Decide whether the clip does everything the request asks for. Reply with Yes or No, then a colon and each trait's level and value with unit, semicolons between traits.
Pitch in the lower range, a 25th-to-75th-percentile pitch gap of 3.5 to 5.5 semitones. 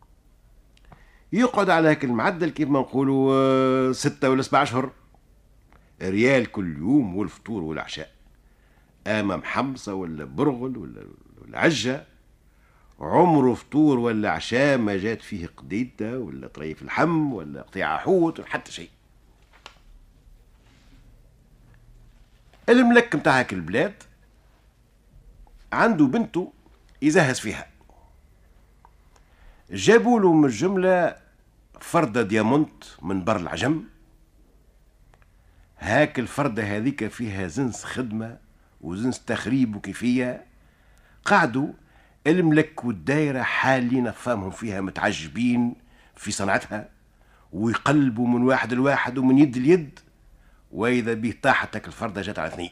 Yes: low, 125 Hz; average, 5.2 semitones